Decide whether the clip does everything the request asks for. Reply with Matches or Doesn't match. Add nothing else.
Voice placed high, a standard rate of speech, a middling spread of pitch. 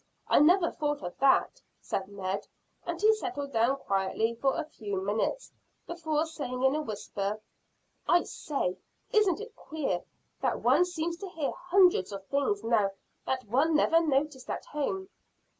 Doesn't match